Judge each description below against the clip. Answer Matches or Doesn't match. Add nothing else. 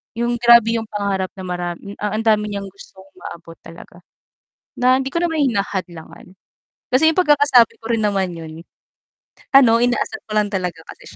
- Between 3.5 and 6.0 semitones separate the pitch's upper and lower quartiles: Matches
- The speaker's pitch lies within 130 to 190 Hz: Doesn't match